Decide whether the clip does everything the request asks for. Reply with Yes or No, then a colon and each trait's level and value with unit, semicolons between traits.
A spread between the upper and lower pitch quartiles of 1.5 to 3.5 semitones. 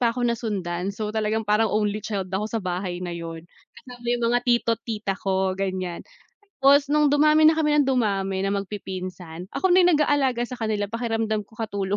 No: average, 4.1 semitones